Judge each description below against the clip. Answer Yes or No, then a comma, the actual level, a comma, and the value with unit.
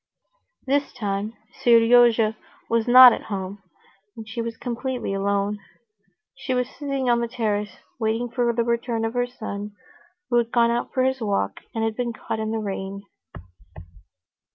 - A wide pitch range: No, narrow, 2.6 semitones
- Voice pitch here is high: Yes, high, 230 Hz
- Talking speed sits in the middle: Yes, average, 155 wpm